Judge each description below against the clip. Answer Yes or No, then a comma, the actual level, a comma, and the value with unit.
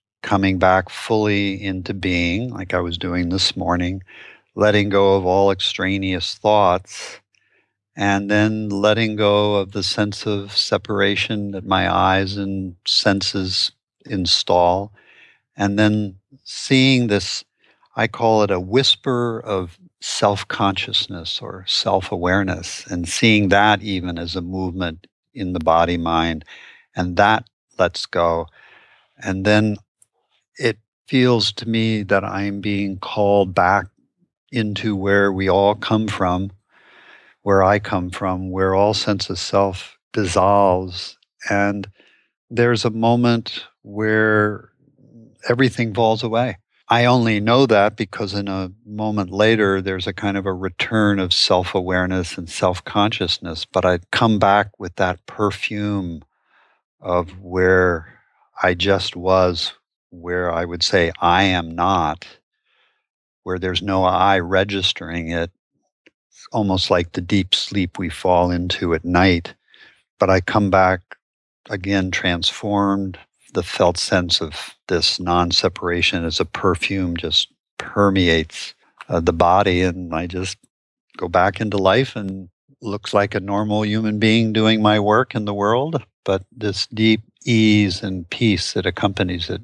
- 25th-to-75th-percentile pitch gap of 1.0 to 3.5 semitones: Yes, narrow, 2.5 semitones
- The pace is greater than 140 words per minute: No, slow, 135 wpm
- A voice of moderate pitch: No, low, 100 Hz